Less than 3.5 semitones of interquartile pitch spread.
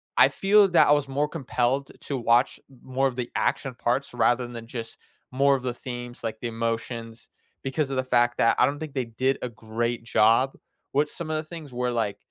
Yes: average, 2.8 semitones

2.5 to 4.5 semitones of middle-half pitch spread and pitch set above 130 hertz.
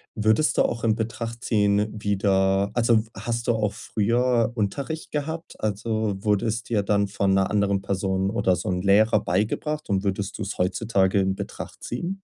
No: average, 2.9 semitones; low, 105 Hz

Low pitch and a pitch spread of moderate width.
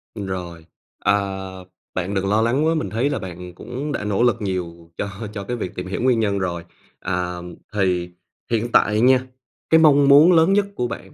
No: low, 105 Hz; wide, 5.9 semitones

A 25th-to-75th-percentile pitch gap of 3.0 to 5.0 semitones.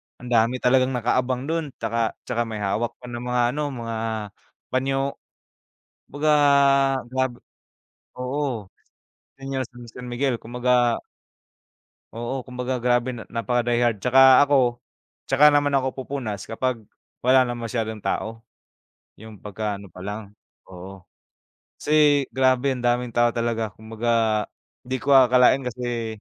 No: narrow, 2.4 semitones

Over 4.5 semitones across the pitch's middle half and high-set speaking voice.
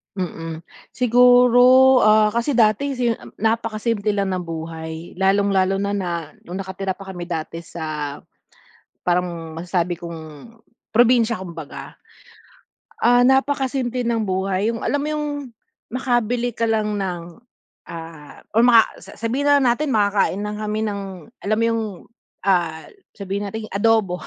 Yes: average, 5.0 semitones; high, 205 Hz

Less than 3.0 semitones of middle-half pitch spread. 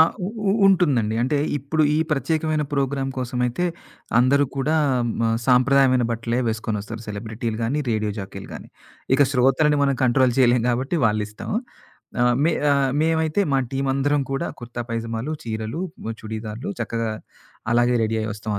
No: average, 3.8 semitones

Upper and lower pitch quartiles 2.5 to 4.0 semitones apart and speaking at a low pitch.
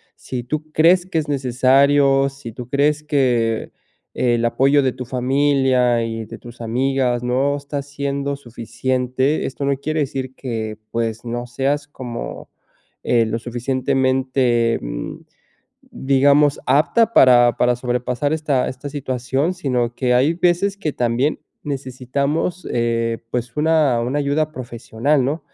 Yes: average, 2.8 semitones; low, 130 Hz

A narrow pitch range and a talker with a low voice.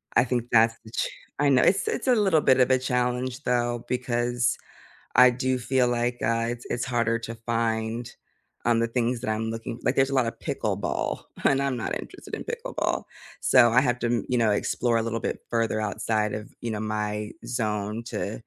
Yes: narrow, 1.8 semitones; low, 120 Hz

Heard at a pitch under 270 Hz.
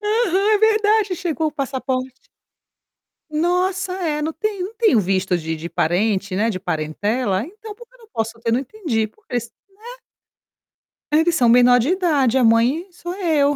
No: very high, 290 Hz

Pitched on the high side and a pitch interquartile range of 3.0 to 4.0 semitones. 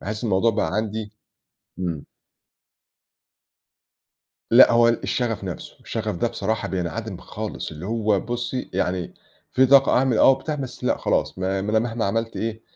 No: low, 110 Hz; average, 3.3 semitones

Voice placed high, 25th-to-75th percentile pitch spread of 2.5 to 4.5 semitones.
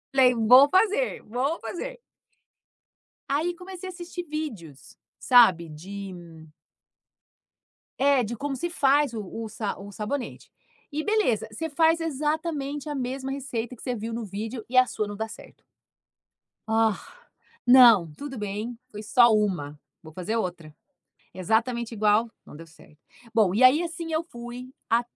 No: high, 240 Hz; wide, 5.6 semitones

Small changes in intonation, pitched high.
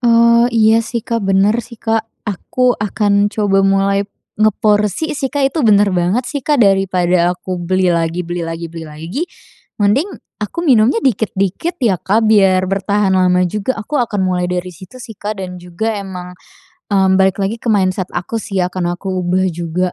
No: average, 3.5 semitones; high, 195 Hz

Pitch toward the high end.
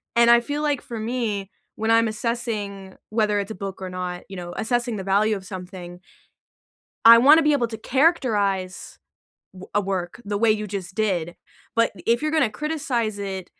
Yes: high, 215 Hz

